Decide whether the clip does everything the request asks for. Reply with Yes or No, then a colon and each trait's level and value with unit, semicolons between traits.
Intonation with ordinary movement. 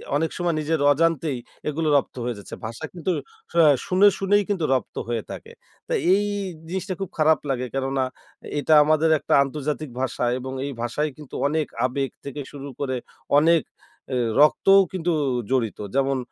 Yes: average, 3.8 semitones